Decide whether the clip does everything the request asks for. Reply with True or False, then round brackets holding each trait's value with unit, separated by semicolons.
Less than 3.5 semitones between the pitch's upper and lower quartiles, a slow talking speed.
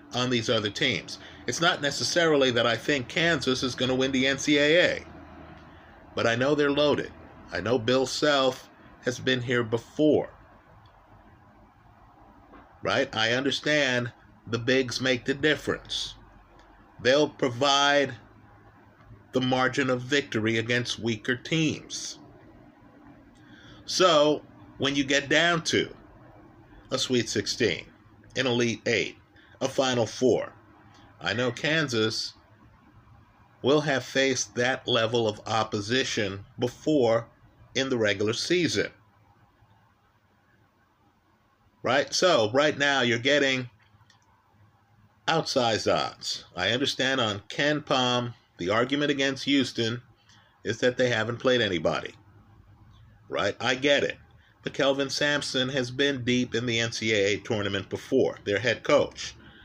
False (3.9 semitones; 120 wpm)